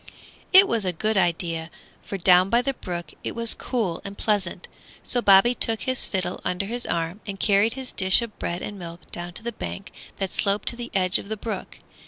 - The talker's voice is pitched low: No, high, 200 Hz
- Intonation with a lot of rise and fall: No, average, 4.2 semitones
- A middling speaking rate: No, fast, 215 wpm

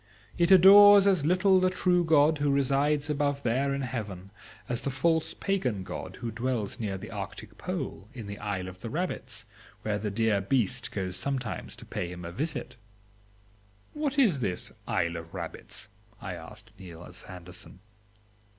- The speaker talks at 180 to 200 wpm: No, average, 165 wpm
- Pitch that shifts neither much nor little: No, wide, 7.9 semitones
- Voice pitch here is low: Yes, low, 125 Hz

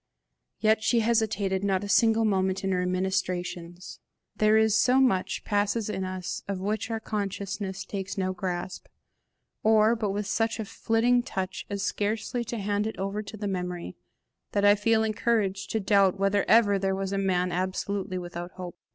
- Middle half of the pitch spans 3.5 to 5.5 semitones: No, narrow, 2.4 semitones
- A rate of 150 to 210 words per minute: Yes, average, 175 wpm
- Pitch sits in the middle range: No, high, 200 Hz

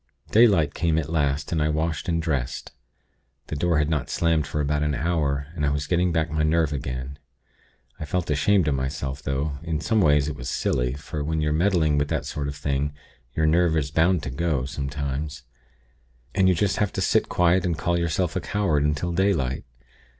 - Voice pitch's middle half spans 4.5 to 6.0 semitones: No, average, 3.0 semitones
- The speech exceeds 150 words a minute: Yes, average, 200 wpm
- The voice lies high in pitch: No, very low, 75 Hz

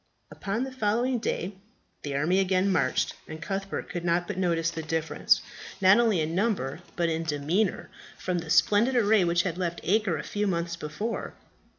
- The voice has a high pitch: No, medium, 180 Hz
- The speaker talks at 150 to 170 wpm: No, average, 180 wpm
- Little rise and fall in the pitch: No, average, 3.8 semitones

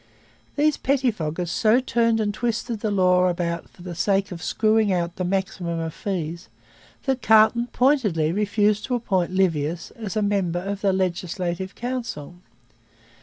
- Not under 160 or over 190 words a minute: No, average, 150 wpm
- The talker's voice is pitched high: Yes, high, 195 Hz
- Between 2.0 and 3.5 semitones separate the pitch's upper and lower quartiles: No, average, 4.0 semitones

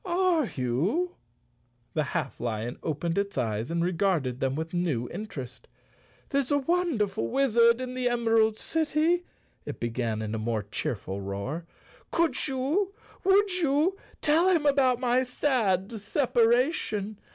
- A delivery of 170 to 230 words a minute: No, average, 145 wpm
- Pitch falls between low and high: No, high, 220 Hz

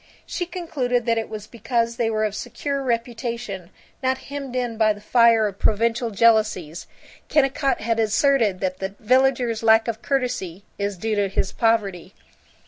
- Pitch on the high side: Yes, high, 230 Hz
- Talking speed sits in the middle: Yes, average, 160 wpm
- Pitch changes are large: No, average, 3.0 semitones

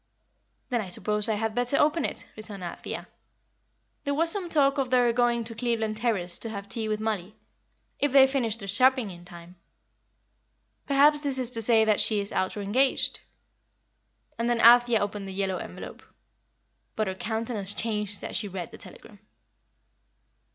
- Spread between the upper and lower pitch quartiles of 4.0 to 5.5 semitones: No, average, 3.4 semitones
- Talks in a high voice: Yes, high, 225 Hz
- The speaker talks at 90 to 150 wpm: No, average, 170 wpm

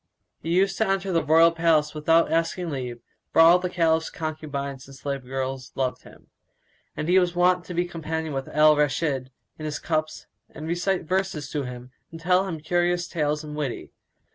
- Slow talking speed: No, average, 190 wpm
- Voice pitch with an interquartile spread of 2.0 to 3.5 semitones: Yes, average, 3.1 semitones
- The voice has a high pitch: No, medium, 160 Hz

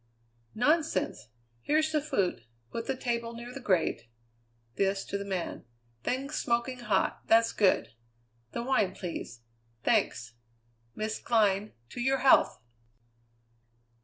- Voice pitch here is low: No, high, 230 Hz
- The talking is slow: Yes, slow, 120 wpm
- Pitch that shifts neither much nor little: Yes, average, 5.0 semitones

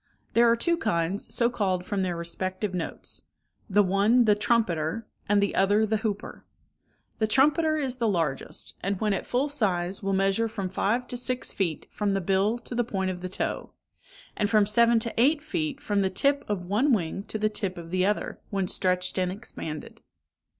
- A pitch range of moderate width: Yes, average, 4.0 semitones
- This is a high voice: Yes, high, 205 Hz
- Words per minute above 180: Yes, average, 190 wpm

